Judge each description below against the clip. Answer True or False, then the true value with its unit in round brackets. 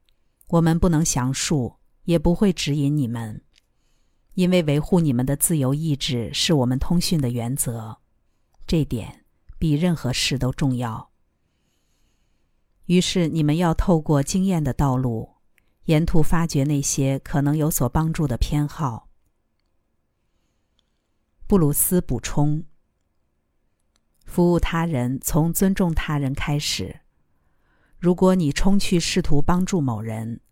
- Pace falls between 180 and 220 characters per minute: True (185 characters per minute)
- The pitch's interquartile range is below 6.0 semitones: False (6.3 semitones)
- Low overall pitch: False (145 Hz)